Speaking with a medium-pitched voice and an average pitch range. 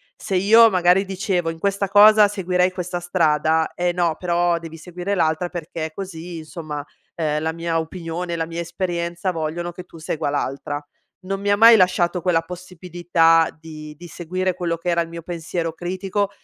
No: medium, 175 Hz; narrow, 2.0 semitones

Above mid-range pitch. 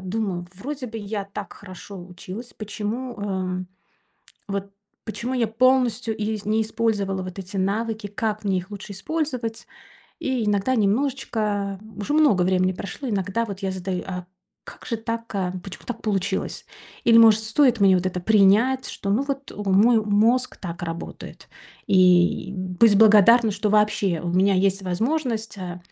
Yes: high, 205 Hz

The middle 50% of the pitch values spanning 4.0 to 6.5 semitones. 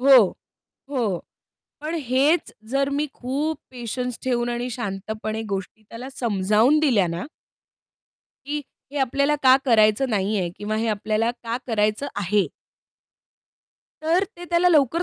Yes: average, 4.6 semitones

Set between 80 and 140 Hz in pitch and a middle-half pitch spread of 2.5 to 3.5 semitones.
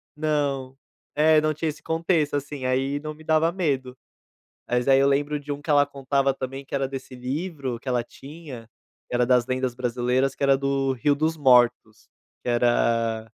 Yes: low, 135 Hz; average, 2.8 semitones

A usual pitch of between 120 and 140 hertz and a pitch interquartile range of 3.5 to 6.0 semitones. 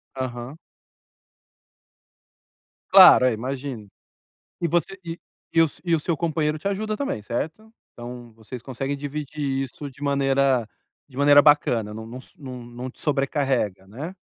Yes: low, 135 Hz; average, 3.8 semitones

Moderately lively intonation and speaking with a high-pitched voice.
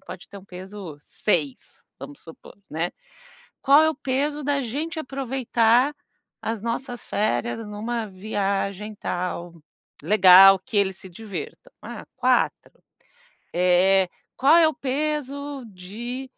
No: wide, 6.0 semitones; high, 220 Hz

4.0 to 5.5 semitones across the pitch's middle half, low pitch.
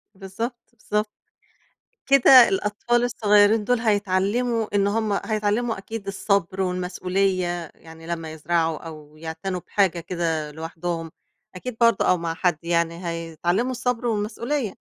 No: average, 4.7 semitones; high, 195 Hz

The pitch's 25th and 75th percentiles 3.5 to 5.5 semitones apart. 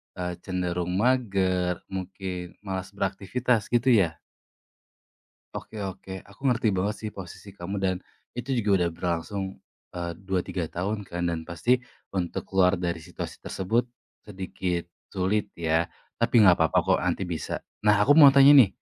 No: average, 3.0 semitones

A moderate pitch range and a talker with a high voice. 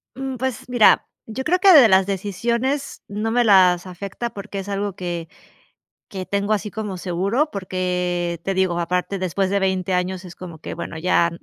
Yes: average, 3.3 semitones; high, 195 Hz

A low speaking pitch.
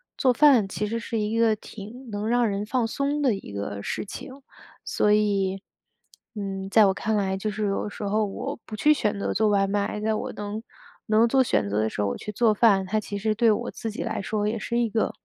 No: high, 215 Hz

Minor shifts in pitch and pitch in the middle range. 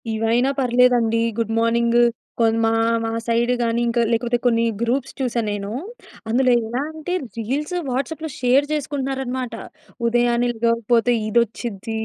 No: narrow, 1.8 semitones; high, 240 Hz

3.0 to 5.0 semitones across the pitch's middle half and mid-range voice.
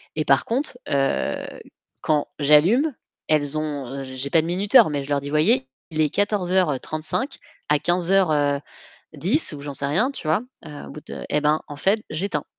Yes: average, 4.2 semitones; medium, 155 Hz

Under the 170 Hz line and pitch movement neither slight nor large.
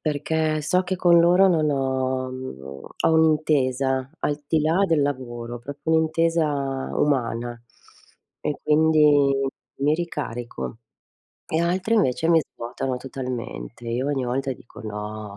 Yes: medium, 140 Hz; average, 4.1 semitones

